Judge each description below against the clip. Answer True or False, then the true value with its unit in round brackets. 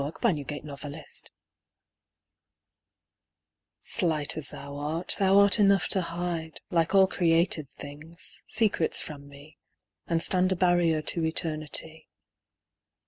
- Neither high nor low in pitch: True (165 Hz)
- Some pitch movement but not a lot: True (3.0 semitones)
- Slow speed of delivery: True (125 wpm)